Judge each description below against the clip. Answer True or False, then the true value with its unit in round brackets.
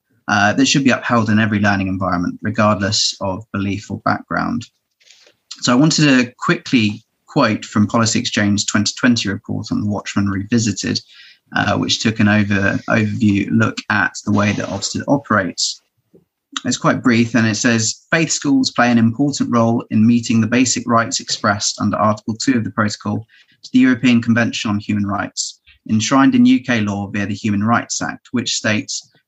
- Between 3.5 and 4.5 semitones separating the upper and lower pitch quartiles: False (2.7 semitones)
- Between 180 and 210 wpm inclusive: False (170 wpm)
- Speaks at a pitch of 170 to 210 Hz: False (110 Hz)